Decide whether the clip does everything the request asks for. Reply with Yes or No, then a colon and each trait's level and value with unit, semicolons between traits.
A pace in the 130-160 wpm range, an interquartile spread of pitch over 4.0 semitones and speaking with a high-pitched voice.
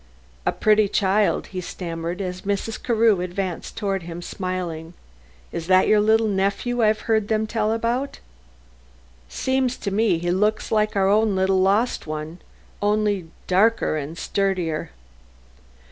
No: average, 140 wpm; average, 3.1 semitones; high, 200 Hz